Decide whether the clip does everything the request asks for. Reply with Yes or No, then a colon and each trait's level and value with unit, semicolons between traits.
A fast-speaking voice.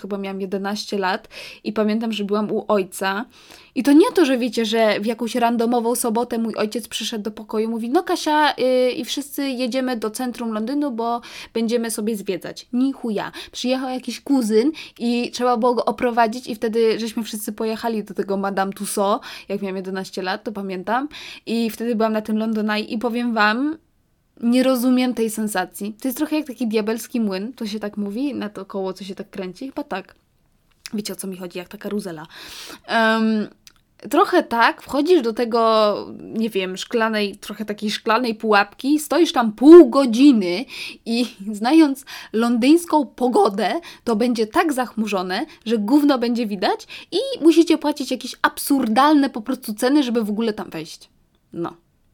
Yes: fast, 170 wpm